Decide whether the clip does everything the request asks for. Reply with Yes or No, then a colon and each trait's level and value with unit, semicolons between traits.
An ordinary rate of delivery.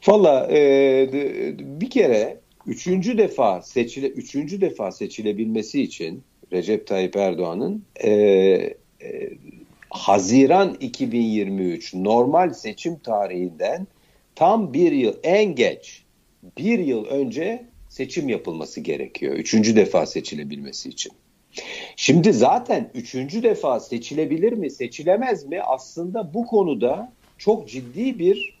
Yes: average, 105 wpm